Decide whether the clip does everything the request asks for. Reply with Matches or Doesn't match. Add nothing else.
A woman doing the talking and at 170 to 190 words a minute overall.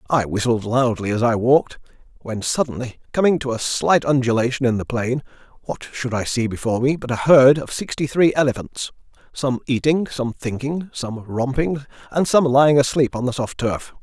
Doesn't match